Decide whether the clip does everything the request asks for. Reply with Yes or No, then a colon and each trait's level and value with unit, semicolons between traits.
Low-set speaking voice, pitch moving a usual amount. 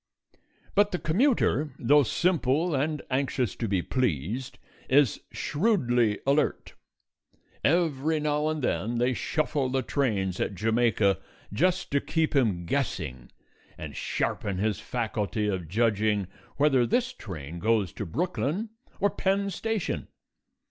No: low, 130 Hz; wide, 6.8 semitones